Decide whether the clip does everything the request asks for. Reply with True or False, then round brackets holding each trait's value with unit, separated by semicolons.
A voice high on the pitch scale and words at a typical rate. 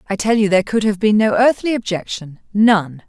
True (205 Hz; 195 wpm)